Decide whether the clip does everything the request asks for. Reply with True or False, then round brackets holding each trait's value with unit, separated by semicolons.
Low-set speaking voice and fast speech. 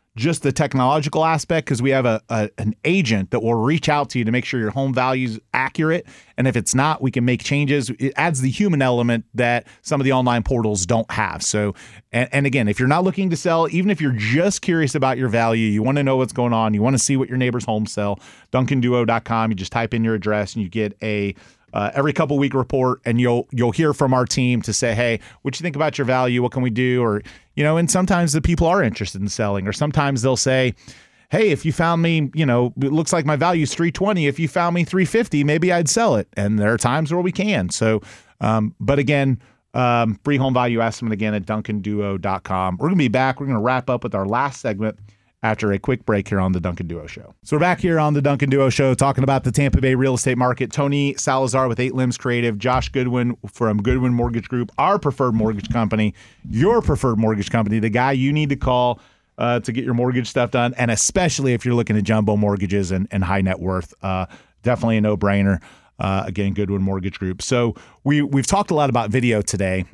True (125 Hz; 235 wpm)